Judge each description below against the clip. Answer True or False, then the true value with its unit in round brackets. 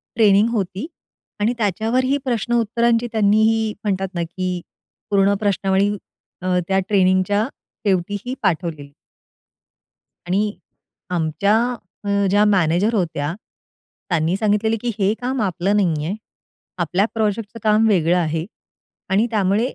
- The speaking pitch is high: True (200 Hz)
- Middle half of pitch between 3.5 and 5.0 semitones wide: False (3.1 semitones)